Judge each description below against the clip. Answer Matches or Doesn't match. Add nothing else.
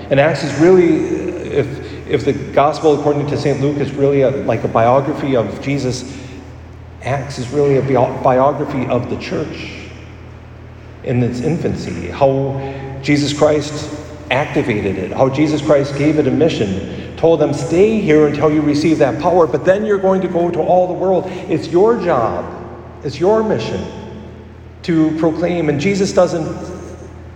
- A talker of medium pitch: Matches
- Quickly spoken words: Doesn't match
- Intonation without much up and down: Doesn't match